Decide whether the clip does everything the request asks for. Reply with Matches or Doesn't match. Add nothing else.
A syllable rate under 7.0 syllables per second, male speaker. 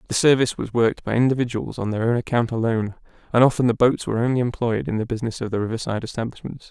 Doesn't match